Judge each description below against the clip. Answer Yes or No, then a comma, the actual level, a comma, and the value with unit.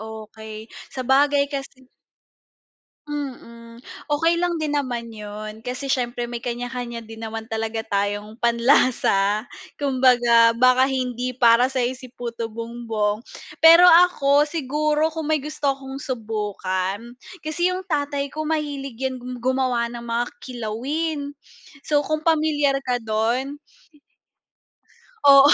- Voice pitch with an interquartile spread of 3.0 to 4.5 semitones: Yes, average, 3.8 semitones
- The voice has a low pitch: No, very high, 255 Hz